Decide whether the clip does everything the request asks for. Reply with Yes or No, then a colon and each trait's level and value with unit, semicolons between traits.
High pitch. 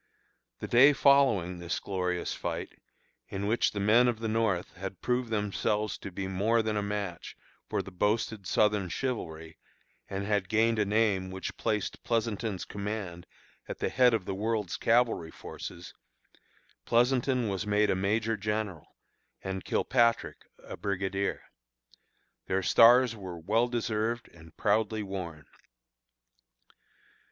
No: low, 105 Hz